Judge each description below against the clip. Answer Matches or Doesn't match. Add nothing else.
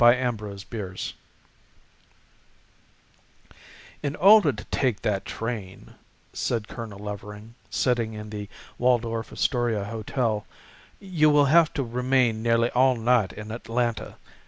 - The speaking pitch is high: Doesn't match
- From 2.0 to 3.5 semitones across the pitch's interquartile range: Matches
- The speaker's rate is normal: Doesn't match